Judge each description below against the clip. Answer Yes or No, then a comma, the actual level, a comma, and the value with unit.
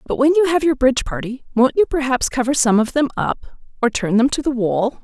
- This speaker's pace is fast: Yes, fast, 250 wpm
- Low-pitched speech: No, very high, 260 Hz